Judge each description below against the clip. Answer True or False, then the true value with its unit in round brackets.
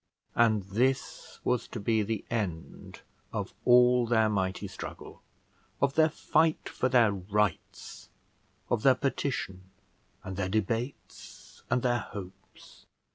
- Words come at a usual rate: False (125 wpm)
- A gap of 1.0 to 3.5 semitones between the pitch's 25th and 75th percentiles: False (4.0 semitones)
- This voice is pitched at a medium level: False (115 Hz)